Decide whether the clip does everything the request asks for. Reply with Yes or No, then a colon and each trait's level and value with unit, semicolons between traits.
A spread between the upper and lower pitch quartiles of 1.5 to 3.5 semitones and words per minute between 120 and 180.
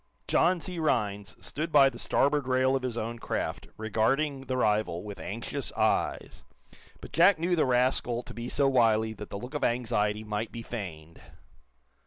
No: average, 4.1 semitones; average, 175 wpm